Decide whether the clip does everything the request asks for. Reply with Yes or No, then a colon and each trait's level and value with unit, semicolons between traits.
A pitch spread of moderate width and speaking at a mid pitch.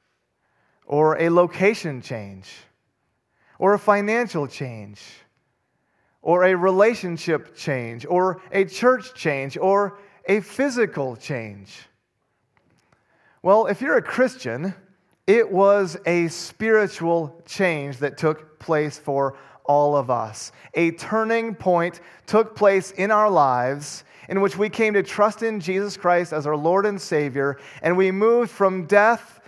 No: wide, 5.8 semitones; medium, 180 Hz